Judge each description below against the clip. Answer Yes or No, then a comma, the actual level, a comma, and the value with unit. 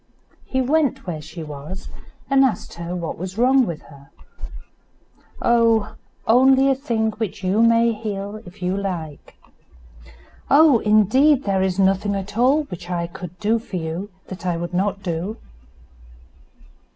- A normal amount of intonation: Yes, average, 4.6 semitones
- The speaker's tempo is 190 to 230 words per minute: No, average, 150 wpm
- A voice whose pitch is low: No, high, 200 Hz